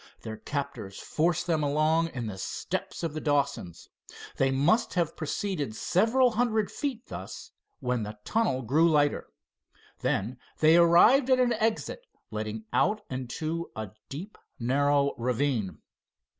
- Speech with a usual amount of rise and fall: No, wide, 6.7 semitones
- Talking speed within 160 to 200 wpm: No, slow, 135 wpm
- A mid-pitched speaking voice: Yes, medium, 150 Hz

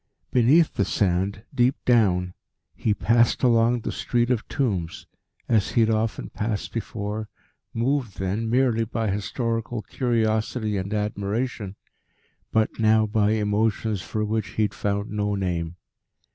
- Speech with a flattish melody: Yes, narrow, 2.2 semitones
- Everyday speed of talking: No, slow, 130 wpm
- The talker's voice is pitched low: Yes, low, 110 Hz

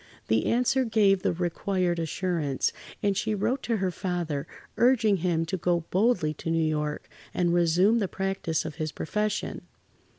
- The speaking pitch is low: No, medium, 180 Hz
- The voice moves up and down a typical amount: Yes, average, 4.2 semitones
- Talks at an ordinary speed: Yes, average, 160 wpm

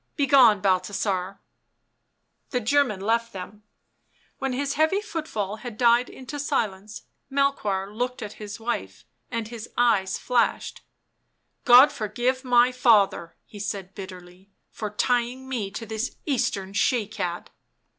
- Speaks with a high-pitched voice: Yes, high, 225 Hz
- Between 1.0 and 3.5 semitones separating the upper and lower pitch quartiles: No, average, 4.1 semitones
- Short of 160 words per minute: Yes, slow, 135 wpm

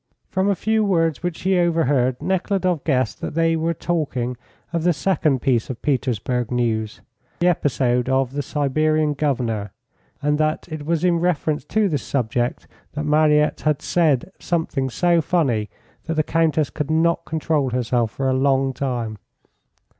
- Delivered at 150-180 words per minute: Yes, average, 160 wpm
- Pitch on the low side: No, medium, 150 Hz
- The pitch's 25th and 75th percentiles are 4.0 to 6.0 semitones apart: Yes, average, 4.3 semitones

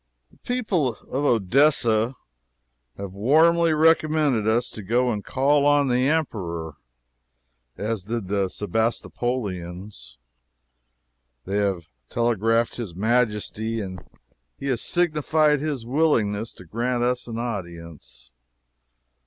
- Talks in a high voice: No, low, 115 Hz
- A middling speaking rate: No, slow, 110 wpm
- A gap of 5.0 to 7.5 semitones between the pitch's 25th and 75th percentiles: Yes, wide, 5.5 semitones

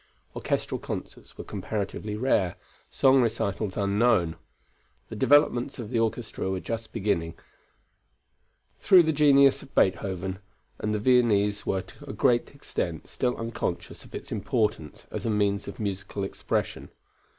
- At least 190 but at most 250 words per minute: No, average, 140 wpm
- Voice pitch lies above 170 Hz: No, low, 105 Hz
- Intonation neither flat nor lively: Yes, average, 3.7 semitones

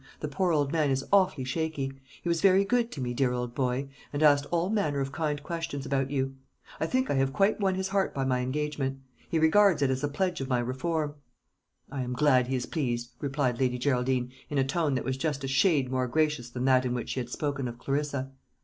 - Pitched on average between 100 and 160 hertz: Yes, medium, 140 Hz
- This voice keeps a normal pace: No, fast, 235 wpm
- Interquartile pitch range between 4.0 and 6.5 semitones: No, average, 3.6 semitones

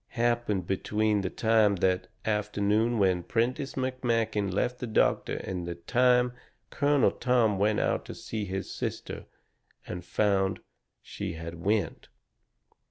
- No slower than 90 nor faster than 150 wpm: Yes, average, 140 wpm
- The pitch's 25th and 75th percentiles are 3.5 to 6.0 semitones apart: Yes, average, 3.8 semitones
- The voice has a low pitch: Yes, low, 105 Hz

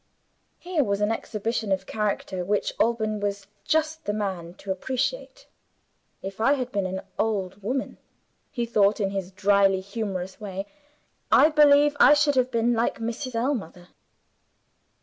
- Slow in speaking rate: No, average, 150 wpm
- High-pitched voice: Yes, high, 215 Hz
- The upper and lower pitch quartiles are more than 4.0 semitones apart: Yes, average, 4.5 semitones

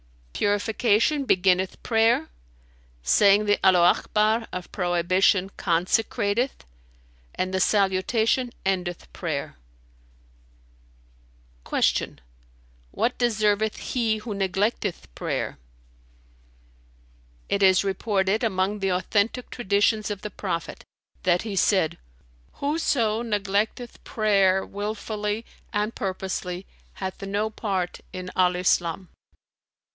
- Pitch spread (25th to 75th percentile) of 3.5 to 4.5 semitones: No, average, 2.7 semitones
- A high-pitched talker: Yes, high, 200 Hz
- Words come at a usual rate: No, slow, 95 wpm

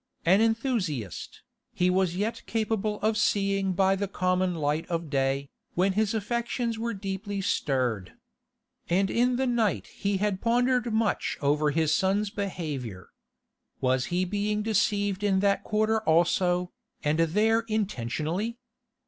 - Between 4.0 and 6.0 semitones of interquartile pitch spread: Yes, average, 4.5 semitones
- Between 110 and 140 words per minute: Yes, slow, 135 wpm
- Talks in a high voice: Yes, high, 195 Hz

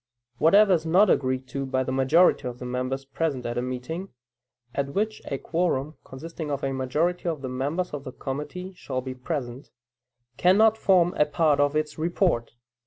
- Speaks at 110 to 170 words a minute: No, average, 180 wpm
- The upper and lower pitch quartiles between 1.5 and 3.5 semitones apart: No, average, 4.8 semitones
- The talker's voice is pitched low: No, medium, 145 Hz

